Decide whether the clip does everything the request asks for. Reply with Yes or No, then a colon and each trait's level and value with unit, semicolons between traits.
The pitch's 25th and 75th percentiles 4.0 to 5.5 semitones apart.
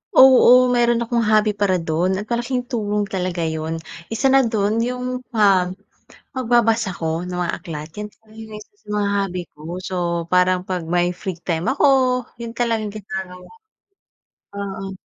Yes: average, 4.5 semitones